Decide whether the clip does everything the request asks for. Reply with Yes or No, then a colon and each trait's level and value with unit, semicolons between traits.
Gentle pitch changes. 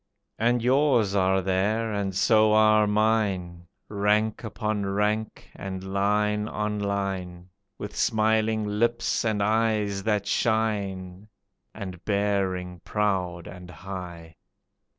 Yes: narrow, 2.2 semitones